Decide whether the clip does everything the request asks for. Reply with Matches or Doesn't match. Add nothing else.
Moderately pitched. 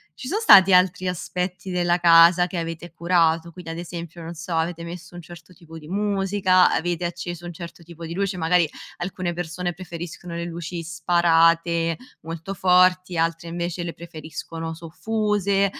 Matches